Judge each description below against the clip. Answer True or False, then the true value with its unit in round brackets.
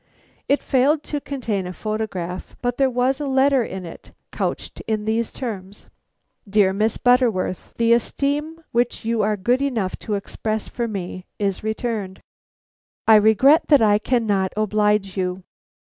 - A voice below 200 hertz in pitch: False (220 Hz)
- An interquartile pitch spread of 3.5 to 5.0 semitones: True (4.0 semitones)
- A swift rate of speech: False (150 wpm)